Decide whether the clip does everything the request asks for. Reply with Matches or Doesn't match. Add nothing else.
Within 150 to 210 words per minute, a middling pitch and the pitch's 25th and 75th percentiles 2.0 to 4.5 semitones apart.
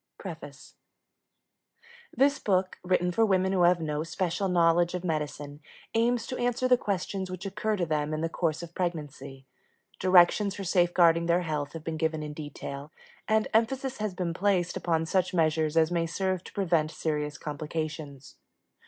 Matches